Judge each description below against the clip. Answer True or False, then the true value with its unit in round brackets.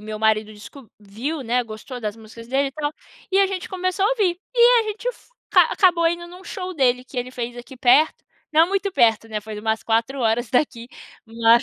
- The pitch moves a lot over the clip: True (7.8 semitones)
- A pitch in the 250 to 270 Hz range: True (255 Hz)